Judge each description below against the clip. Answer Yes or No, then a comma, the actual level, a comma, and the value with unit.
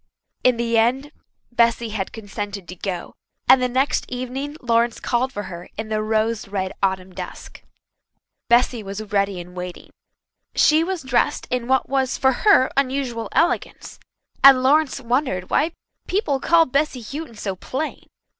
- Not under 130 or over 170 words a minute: Yes, average, 155 wpm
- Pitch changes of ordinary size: Yes, average, 4.5 semitones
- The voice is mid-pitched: No, high, 240 Hz